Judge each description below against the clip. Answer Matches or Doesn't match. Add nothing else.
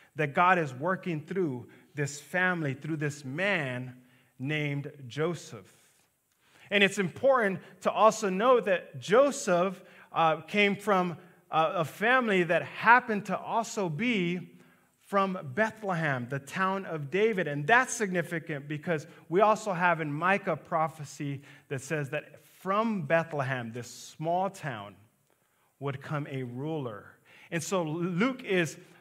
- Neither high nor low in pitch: Matches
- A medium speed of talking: Doesn't match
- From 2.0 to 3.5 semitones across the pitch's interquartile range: Doesn't match